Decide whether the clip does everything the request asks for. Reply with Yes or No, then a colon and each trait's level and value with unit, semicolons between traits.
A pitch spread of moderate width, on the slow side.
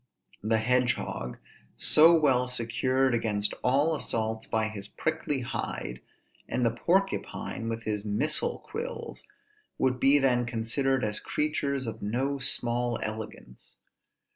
Yes: average, 3.7 semitones; slow, 125 wpm